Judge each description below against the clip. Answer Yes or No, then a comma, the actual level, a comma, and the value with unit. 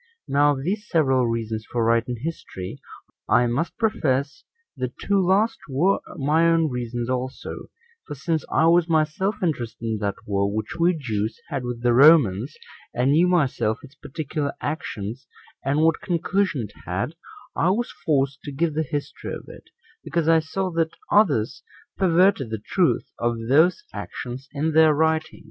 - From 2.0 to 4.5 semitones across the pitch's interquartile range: No, average, 5.3 semitones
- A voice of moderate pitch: Yes, medium, 145 Hz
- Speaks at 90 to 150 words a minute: No, average, 160 wpm